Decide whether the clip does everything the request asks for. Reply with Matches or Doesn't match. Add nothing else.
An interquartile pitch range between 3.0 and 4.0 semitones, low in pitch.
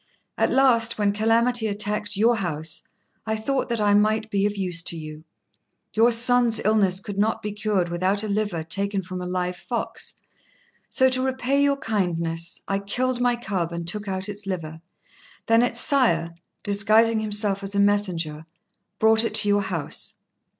Doesn't match